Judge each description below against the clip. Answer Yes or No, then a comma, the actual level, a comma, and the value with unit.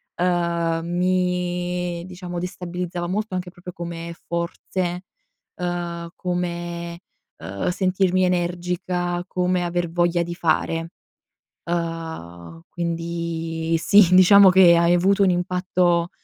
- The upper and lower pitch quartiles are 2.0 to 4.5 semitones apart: No, narrow, 1.1 semitones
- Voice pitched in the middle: Yes, medium, 175 Hz